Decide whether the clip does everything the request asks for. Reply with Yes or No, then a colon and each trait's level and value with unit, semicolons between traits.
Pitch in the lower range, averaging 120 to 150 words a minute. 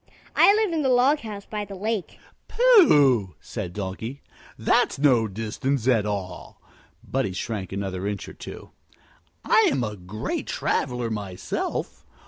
Yes: low, 120 Hz; average, 140 wpm